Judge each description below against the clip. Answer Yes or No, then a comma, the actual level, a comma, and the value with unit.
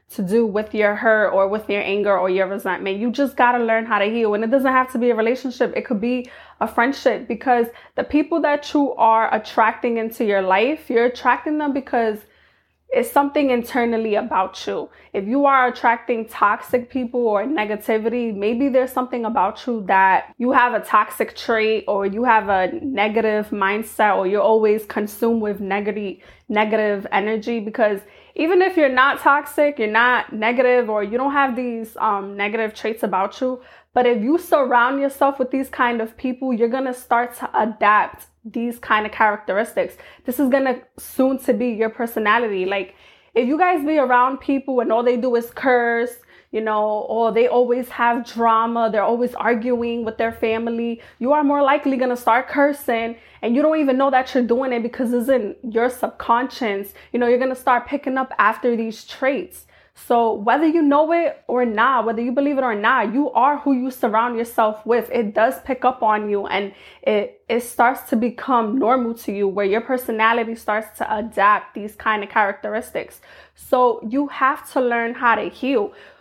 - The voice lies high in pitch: Yes, high, 235 Hz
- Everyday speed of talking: Yes, average, 195 wpm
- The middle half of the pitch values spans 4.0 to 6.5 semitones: No, average, 3.1 semitones